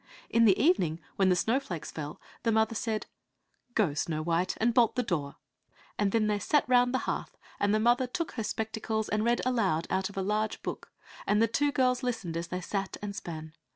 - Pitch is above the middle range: Yes, high, 215 Hz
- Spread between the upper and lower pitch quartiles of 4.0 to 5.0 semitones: Yes, average, 4.7 semitones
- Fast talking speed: Yes, fast, 210 wpm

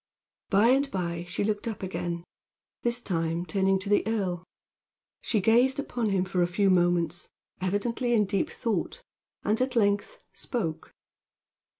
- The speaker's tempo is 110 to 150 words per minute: Yes, average, 145 wpm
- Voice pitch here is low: No, high, 200 Hz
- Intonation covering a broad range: No, average, 4.5 semitones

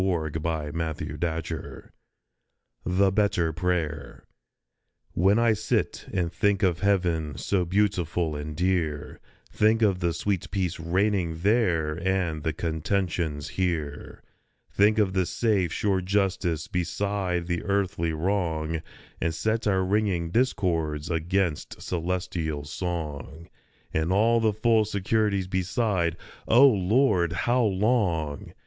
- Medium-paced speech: No, slow, 125 wpm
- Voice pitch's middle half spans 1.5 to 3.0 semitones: No, average, 3.7 semitones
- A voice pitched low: Yes, very low, 90 Hz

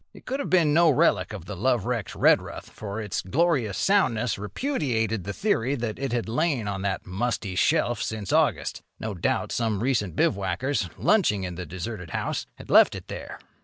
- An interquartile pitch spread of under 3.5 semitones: No, wide, 5.6 semitones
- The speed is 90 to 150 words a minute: No, average, 180 wpm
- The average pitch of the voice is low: Yes, low, 110 Hz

